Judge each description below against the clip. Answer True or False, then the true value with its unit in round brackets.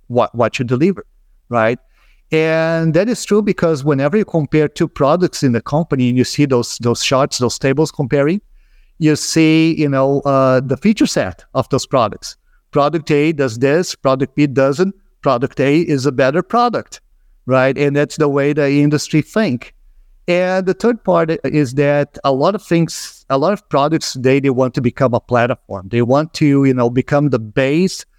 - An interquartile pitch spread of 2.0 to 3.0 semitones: False (3.7 semitones)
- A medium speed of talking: True (185 wpm)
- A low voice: False (145 Hz)